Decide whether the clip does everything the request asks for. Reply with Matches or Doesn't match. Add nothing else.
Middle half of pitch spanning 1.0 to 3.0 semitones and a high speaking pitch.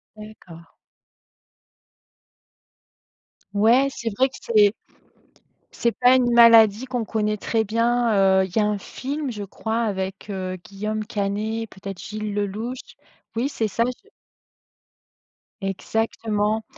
Matches